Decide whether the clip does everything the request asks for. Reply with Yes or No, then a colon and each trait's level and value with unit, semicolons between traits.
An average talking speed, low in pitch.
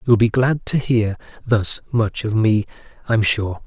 No: fast, 215 wpm; low, 110 Hz